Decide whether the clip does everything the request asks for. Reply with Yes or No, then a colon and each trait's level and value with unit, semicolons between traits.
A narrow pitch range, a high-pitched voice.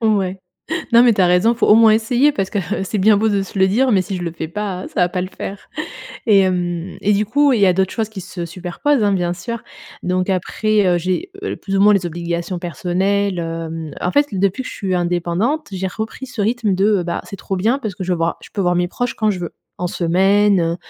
No: average, 3.3 semitones; high, 195 Hz